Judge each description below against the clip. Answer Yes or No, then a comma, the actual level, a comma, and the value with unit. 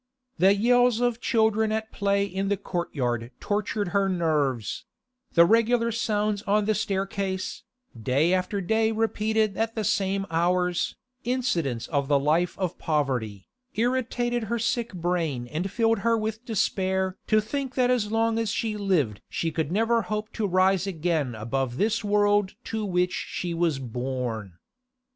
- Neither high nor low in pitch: No, high, 195 Hz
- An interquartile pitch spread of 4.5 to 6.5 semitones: Yes, average, 5.0 semitones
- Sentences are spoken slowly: No, average, 155 wpm